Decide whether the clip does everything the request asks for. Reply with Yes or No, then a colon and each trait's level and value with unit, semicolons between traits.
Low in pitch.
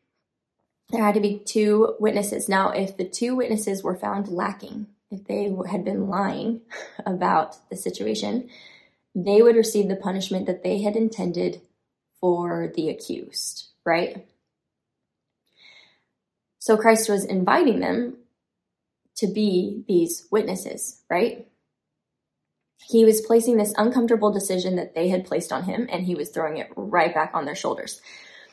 No: high, 205 Hz